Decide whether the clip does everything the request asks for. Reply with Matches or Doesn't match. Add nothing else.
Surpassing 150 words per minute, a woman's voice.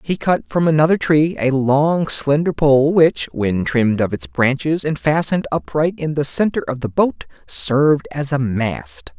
Doesn't match